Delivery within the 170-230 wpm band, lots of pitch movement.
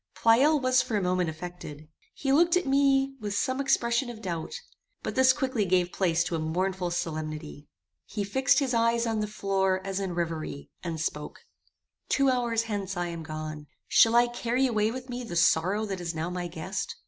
Yes: average, 195 wpm; wide, 6.2 semitones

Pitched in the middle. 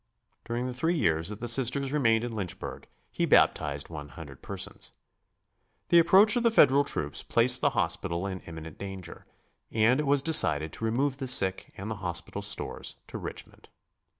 No: low, 115 Hz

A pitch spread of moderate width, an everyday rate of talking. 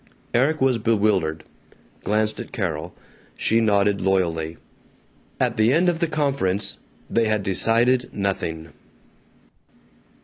No: average, 4.3 semitones; slow, 110 wpm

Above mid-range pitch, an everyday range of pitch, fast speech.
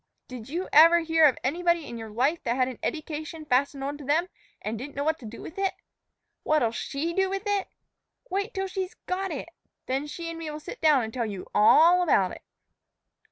Yes: very high, 305 Hz; average, 4.9 semitones; fast, 220 wpm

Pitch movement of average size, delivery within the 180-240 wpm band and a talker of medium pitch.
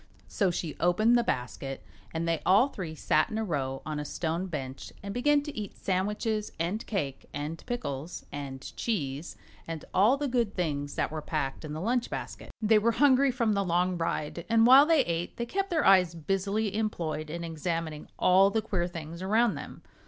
No: wide, 6.0 semitones; average, 195 wpm; medium, 180 Hz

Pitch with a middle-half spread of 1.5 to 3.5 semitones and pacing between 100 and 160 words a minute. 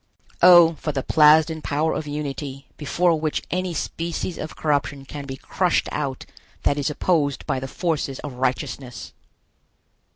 Yes: average, 2.8 semitones; average, 150 wpm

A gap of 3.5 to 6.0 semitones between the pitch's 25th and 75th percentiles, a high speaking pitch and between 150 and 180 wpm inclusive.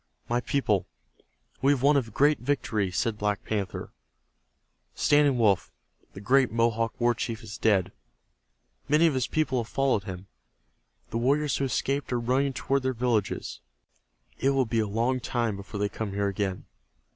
No: average, 4.4 semitones; low, 120 Hz; average, 165 wpm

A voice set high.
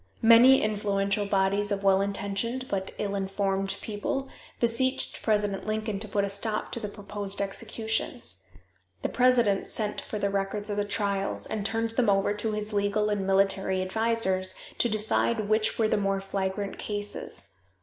Yes: high, 205 Hz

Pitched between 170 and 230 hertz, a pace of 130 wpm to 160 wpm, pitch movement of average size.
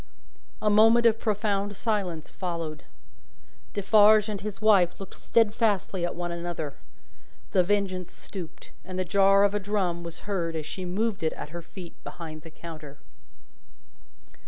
Yes: high, 190 Hz; average, 150 wpm; average, 3.4 semitones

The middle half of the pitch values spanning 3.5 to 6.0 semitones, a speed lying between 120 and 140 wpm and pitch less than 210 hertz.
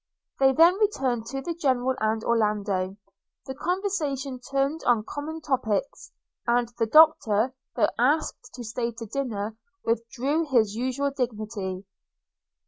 No: average, 4.3 semitones; slow, 135 wpm; very high, 250 Hz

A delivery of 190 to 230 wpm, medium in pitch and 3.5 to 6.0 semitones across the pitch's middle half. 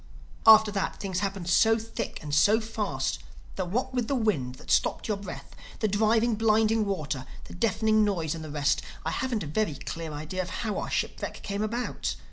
No: average, 195 wpm; high, 205 Hz; average, 5.2 semitones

